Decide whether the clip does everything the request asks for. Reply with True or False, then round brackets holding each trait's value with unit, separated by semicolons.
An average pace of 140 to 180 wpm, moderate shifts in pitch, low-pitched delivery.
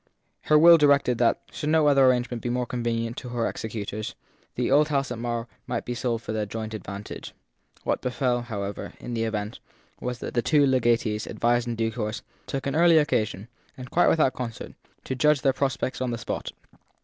False (195 wpm; 3.1 semitones; 120 Hz)